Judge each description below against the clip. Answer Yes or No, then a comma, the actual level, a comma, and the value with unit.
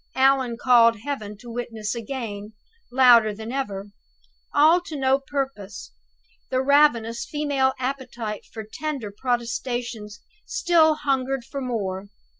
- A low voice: No, very high, 250 Hz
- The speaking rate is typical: No, slow, 115 wpm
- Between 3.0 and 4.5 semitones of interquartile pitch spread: Yes, average, 3.7 semitones